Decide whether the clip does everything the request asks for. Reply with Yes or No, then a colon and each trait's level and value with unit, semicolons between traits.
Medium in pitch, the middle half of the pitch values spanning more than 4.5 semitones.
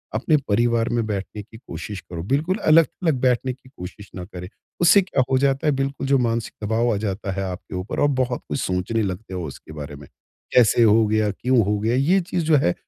No: low, 115 Hz; average, 5.2 semitones